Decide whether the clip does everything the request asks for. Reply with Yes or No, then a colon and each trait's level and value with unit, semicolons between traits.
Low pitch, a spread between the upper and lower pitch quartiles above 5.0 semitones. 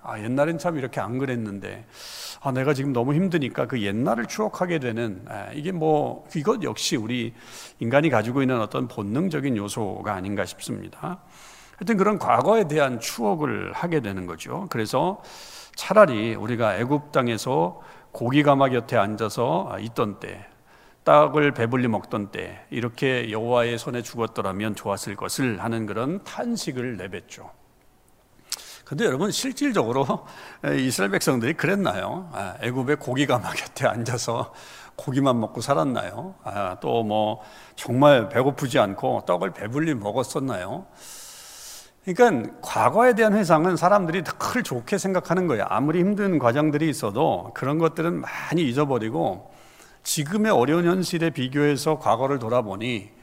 Yes: low, 130 Hz; wide, 5.6 semitones